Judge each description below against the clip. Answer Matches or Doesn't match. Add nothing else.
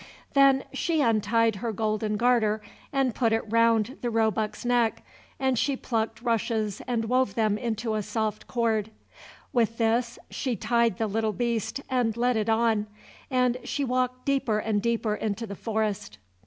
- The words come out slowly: Doesn't match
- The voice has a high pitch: Matches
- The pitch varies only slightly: Matches